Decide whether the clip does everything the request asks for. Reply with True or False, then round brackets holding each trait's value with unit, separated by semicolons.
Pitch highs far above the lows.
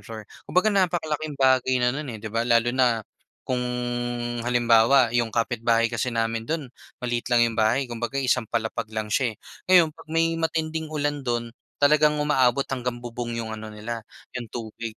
False (3.8 semitones)